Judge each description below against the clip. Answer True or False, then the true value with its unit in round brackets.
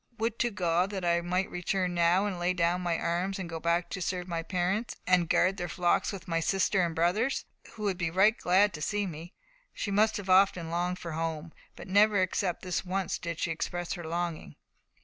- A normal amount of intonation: False (2.3 semitones)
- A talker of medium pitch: True (180 Hz)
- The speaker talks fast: True (220 wpm)